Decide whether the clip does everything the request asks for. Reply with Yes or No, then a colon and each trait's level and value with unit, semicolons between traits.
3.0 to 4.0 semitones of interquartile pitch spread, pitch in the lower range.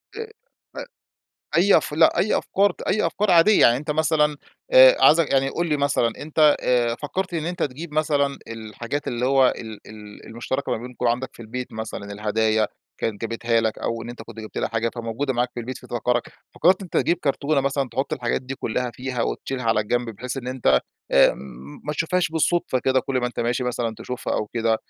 No: average, 4.6 semitones; low, 125 Hz